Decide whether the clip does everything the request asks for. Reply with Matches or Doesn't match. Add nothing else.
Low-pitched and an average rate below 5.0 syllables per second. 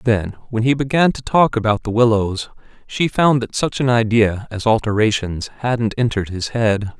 Matches